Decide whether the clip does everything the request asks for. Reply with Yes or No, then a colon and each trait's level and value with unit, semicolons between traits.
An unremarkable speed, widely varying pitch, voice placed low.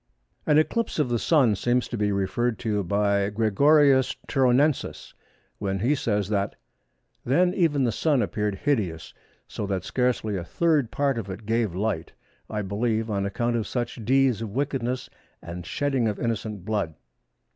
No: average, 155 wpm; average, 4.7 semitones; low, 115 Hz